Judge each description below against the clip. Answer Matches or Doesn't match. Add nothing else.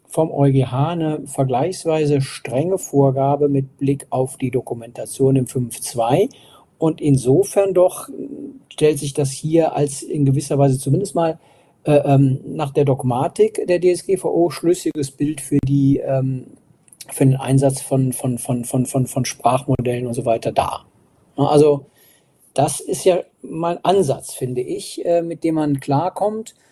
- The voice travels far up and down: Doesn't match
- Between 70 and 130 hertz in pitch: Doesn't match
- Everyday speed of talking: Matches